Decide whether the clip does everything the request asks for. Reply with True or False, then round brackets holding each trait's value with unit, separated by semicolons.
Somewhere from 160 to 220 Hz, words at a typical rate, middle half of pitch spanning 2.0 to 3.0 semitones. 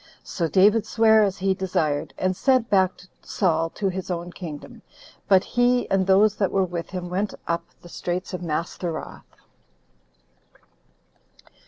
True (185 Hz; 145 wpm; 2.5 semitones)